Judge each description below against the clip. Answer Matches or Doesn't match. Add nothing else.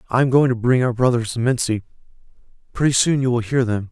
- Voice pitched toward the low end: Matches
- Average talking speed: Doesn't match